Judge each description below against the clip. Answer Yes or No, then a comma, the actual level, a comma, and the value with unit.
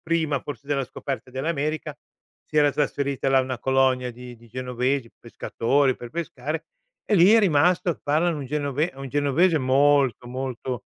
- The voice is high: No, medium, 140 Hz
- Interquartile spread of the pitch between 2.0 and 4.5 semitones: Yes, average, 2.8 semitones